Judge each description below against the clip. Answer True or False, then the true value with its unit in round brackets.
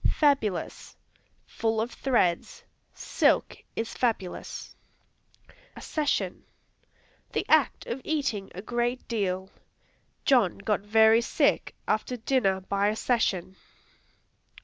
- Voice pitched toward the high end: True (220 Hz)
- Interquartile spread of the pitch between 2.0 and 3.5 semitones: False (4.0 semitones)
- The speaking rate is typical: False (95 wpm)